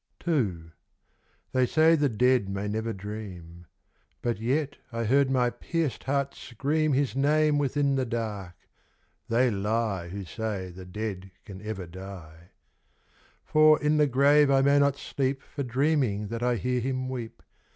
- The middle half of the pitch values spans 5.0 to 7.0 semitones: Yes, wide, 5.6 semitones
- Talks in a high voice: No, low, 120 Hz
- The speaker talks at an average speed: Yes, average, 150 wpm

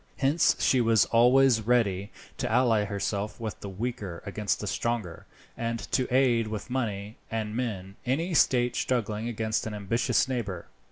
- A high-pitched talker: No, low, 115 Hz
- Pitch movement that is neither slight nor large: Yes, average, 3.1 semitones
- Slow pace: No, average, 155 wpm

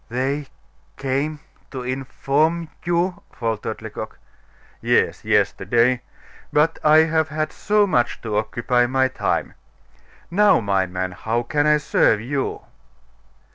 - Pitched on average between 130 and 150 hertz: Yes, low, 135 Hz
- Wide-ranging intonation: No, average, 4.6 semitones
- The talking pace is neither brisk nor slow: No, slow, 125 wpm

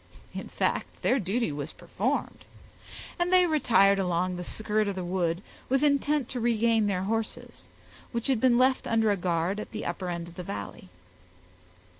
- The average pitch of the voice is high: Yes, high, 210 Hz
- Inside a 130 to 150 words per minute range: No, average, 175 wpm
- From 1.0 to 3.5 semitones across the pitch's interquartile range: No, average, 5.2 semitones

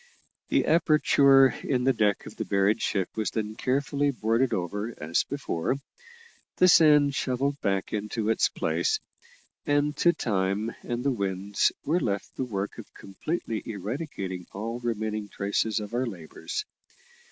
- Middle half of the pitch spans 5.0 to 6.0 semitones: Yes, wide, 5.4 semitones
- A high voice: No, low, 115 Hz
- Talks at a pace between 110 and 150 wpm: Yes, average, 145 wpm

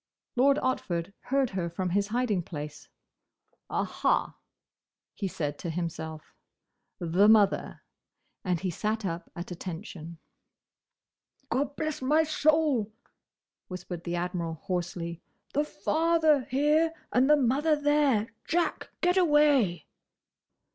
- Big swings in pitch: Yes, wide, 9.0 semitones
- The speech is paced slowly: Yes, slow, 105 wpm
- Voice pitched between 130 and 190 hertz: No, high, 215 Hz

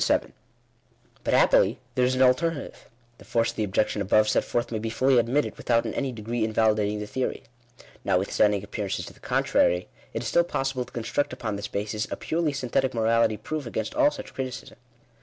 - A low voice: Yes, low, 115 Hz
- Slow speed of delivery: No, average, 195 wpm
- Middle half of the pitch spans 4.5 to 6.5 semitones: No, average, 3.8 semitones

